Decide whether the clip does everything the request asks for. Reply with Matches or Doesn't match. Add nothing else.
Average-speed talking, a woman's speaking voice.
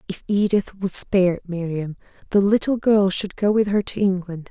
Matches